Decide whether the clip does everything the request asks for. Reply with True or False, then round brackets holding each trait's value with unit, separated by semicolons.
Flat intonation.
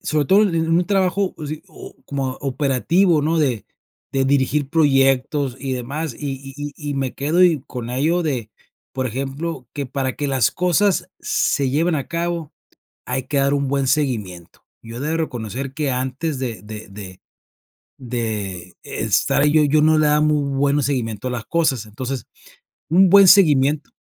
False (3.3 semitones)